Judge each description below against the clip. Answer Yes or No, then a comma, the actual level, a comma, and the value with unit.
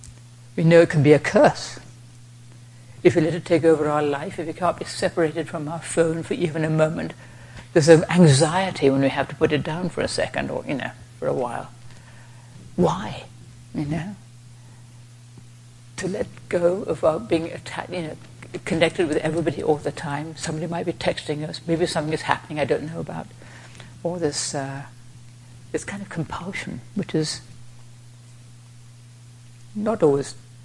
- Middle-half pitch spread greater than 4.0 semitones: Yes, wide, 5.5 semitones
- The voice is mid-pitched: Yes, medium, 145 Hz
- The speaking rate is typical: Yes, average, 170 wpm